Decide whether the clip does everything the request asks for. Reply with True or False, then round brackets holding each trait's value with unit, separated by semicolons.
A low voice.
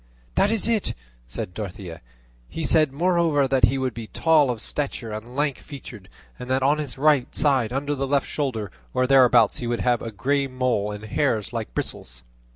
True (130 Hz)